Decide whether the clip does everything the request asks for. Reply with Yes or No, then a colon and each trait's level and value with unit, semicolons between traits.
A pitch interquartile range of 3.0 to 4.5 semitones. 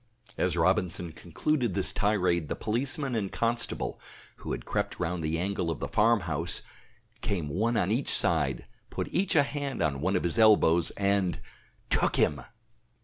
No: average, 5.2 semitones